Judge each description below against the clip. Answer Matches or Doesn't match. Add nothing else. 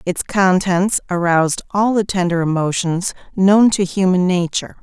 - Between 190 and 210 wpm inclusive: Doesn't match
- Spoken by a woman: Matches